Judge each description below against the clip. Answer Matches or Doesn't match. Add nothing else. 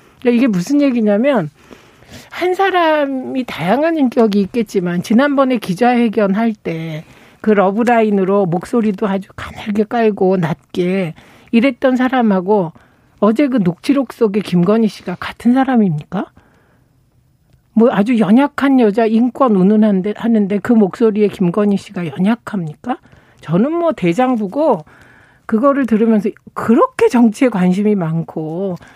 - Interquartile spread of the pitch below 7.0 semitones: Matches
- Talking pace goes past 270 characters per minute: Matches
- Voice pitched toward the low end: Doesn't match